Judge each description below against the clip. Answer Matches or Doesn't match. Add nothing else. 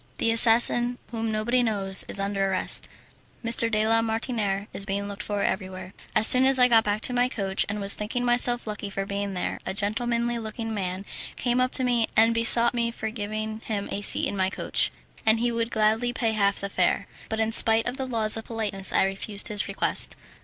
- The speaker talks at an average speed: Doesn't match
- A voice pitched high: Matches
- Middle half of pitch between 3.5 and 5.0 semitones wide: Doesn't match